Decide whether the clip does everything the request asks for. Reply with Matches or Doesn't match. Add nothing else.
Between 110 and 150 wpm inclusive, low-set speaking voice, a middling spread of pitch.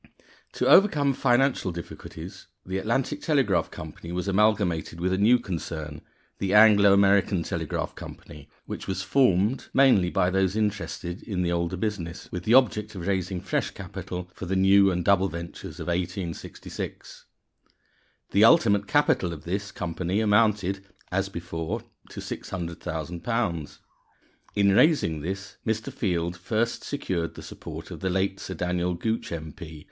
Matches